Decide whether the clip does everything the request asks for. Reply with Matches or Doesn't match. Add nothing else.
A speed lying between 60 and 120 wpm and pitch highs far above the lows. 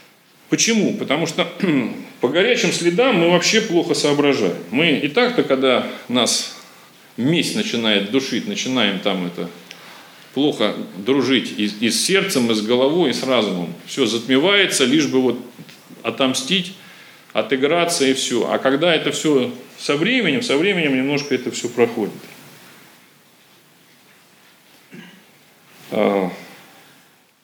Matches